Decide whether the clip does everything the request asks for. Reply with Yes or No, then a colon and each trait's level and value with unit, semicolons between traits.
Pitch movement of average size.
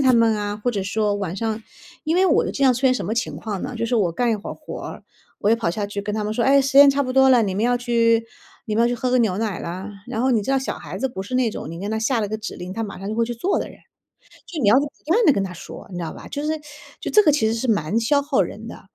Yes: average, 3.9 semitones